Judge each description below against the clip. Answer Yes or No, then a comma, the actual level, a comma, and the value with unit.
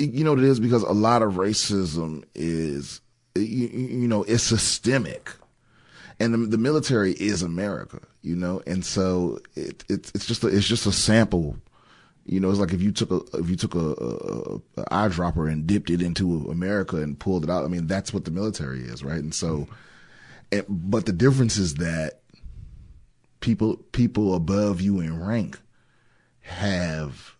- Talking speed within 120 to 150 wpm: No, average, 180 wpm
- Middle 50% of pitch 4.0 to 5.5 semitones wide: Yes, average, 4.9 semitones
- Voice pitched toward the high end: No, very low, 95 Hz